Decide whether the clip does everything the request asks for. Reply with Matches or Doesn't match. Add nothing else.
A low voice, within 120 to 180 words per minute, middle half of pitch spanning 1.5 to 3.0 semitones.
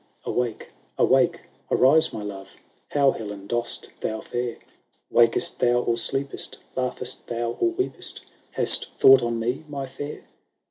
Matches